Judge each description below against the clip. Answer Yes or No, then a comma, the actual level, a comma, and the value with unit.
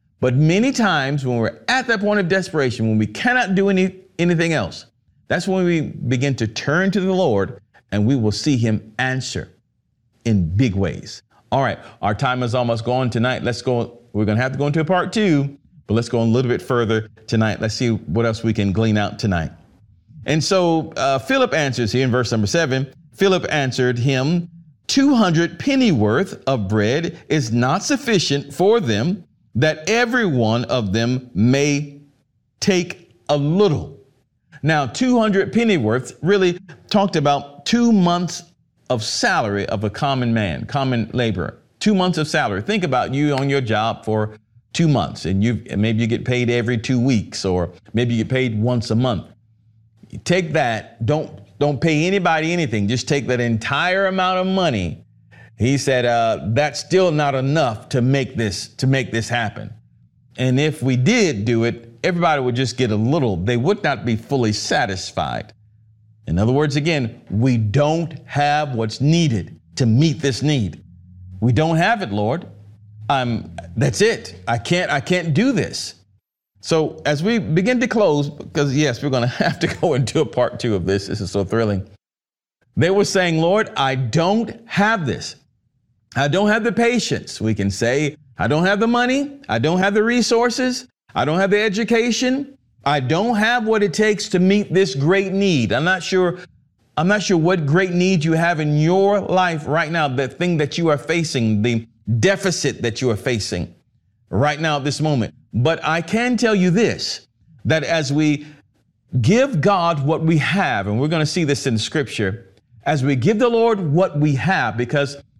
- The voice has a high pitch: No, medium, 140 Hz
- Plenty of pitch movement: Yes, wide, 7.2 semitones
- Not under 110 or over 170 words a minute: No, average, 185 wpm